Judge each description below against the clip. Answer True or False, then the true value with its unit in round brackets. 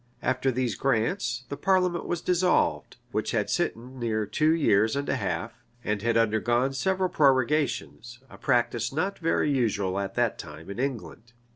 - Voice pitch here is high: False (125 Hz)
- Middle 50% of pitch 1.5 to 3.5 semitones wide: False (4.6 semitones)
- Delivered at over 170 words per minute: False (160 wpm)